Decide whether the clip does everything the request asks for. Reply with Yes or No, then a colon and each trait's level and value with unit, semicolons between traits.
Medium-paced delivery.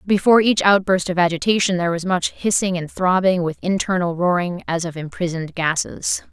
Yes: average, 170 wpm